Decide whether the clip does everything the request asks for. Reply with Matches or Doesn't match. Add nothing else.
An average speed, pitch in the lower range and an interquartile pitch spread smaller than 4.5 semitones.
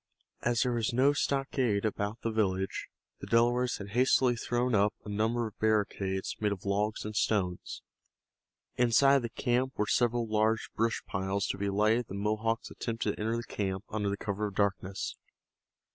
Matches